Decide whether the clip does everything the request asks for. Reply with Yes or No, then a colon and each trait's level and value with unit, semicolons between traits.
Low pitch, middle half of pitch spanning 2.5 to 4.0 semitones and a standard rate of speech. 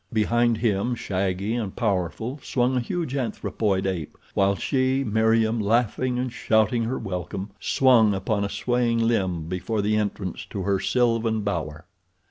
Yes: low, 110 Hz; average, 3.6 semitones; average, 145 wpm